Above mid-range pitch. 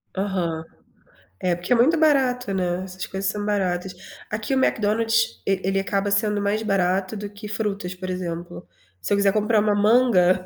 Yes: high, 200 Hz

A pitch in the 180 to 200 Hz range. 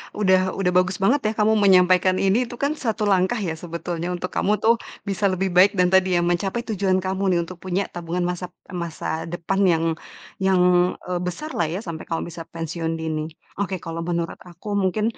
Yes: medium, 185 Hz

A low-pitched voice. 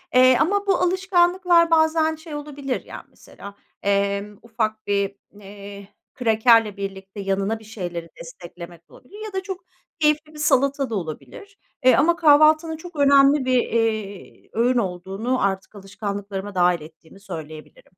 No: high, 225 Hz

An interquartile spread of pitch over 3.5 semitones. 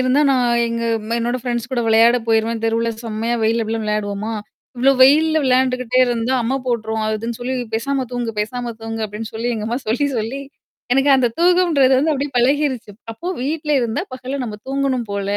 No: average, 2.9 semitones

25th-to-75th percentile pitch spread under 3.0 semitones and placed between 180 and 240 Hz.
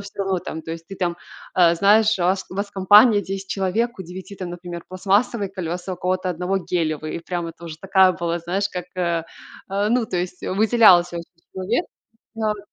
Yes: narrow, 2.5 semitones; medium, 185 Hz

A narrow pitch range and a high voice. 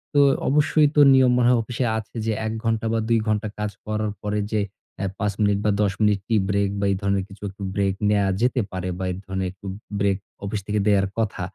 No: narrow, 2.3 semitones; low, 105 Hz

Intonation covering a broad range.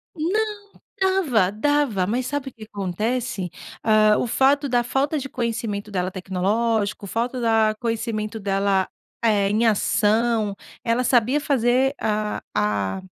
No: average, 3.8 semitones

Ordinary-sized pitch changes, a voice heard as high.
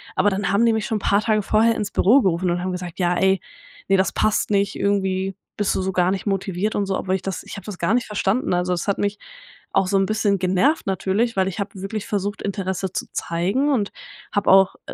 No: narrow, 1.8 semitones; high, 195 Hz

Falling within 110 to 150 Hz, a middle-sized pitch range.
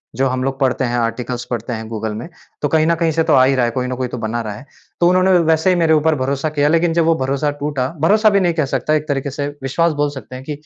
Yes: medium, 140 Hz; average, 4.2 semitones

